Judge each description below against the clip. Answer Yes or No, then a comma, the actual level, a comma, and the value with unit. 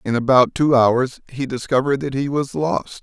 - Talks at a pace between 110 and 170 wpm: No, average, 200 wpm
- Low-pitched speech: Yes, low, 130 Hz